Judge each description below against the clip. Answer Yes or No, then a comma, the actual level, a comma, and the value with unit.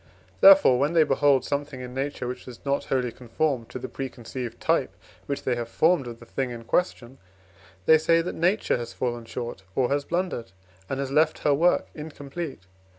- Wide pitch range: No, average, 4.1 semitones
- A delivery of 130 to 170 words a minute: No, average, 190 wpm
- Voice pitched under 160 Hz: Yes, low, 135 Hz